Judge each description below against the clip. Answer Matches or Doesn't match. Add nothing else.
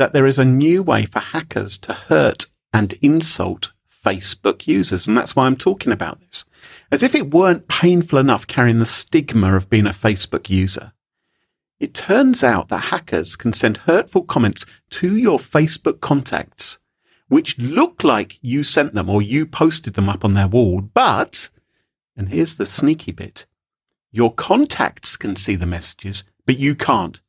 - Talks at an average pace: Matches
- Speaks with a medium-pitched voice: Doesn't match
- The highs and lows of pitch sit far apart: Matches